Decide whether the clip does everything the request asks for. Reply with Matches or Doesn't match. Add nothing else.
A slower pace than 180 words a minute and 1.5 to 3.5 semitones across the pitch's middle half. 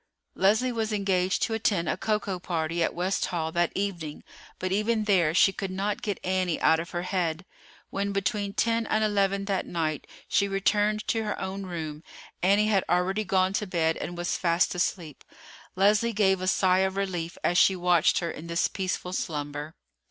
Doesn't match